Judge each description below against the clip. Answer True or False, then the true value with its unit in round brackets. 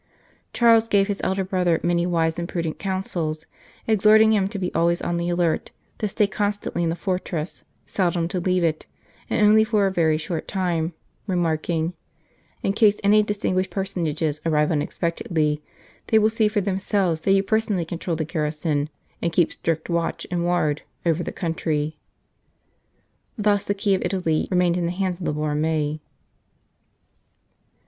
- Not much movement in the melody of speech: False (3.3 semitones)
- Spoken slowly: False (165 wpm)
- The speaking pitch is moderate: True (175 Hz)